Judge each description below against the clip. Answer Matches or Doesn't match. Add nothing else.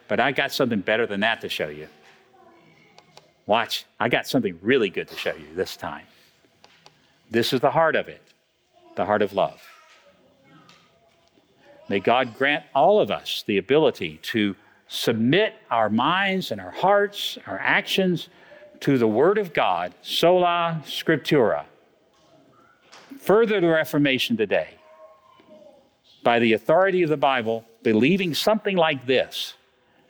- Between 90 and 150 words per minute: Matches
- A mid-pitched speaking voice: Matches